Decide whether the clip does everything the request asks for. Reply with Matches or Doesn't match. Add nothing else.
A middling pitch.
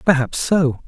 Matches